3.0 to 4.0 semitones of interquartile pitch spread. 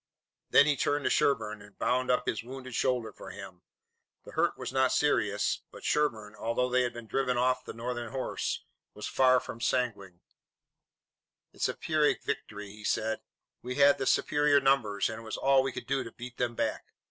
Yes: average, 3.3 semitones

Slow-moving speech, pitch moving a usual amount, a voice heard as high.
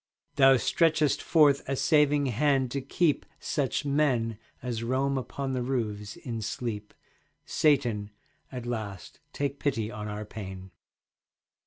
No: slow, 130 wpm; average, 4.4 semitones; low, 130 Hz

